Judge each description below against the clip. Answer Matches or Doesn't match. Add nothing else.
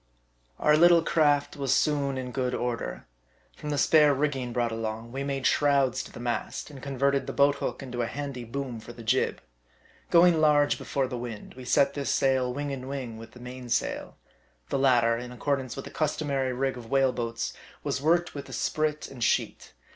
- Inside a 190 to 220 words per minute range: Matches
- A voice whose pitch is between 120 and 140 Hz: Matches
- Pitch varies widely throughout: Doesn't match